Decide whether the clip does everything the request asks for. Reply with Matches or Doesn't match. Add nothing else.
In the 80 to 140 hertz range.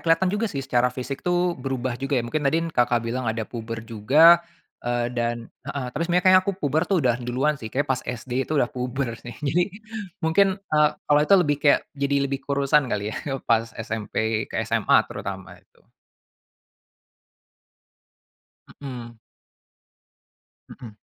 Matches